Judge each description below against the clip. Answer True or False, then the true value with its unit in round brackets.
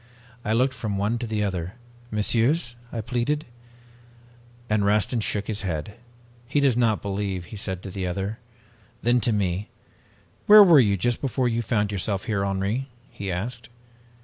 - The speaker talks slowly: False (165 wpm)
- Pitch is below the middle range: True (105 Hz)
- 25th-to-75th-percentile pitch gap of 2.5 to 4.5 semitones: True (3.4 semitones)